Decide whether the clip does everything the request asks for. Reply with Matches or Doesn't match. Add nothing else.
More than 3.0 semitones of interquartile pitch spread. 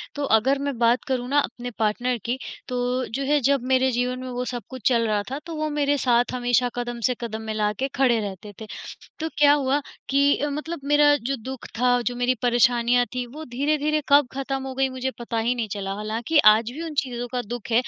Doesn't match